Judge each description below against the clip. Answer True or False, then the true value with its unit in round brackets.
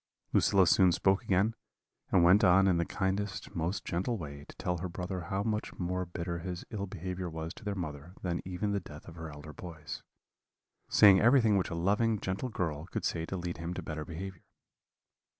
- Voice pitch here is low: True (90 Hz)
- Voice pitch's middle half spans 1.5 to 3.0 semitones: True (2.6 semitones)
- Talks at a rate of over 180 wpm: True (200 wpm)